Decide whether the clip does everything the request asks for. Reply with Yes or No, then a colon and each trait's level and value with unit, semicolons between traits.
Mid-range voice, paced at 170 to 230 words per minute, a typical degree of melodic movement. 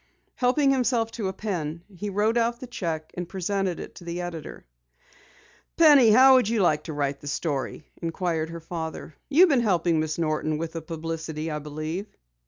No: medium, 175 Hz; average, 185 wpm; wide, 5.9 semitones